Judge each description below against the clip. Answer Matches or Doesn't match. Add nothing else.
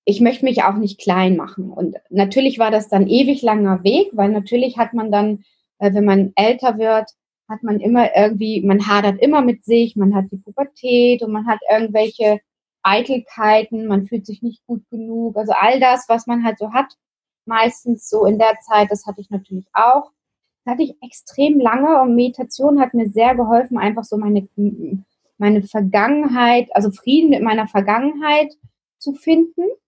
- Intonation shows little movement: Doesn't match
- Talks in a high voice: Matches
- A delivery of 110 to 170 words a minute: Doesn't match